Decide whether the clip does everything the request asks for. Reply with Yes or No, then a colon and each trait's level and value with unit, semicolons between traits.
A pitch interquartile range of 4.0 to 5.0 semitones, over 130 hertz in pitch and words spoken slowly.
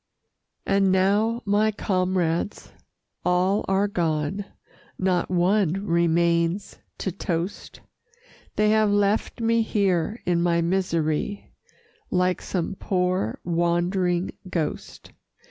No: average, 2.9 semitones; medium, 185 Hz; slow, 95 wpm